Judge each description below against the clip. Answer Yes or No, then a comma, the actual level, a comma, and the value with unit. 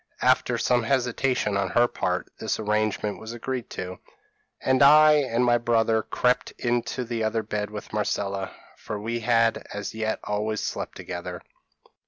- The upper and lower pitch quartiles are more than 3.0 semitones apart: No, narrow, 2.4 semitones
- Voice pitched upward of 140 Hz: No, low, 115 Hz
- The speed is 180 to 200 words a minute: No, average, 155 wpm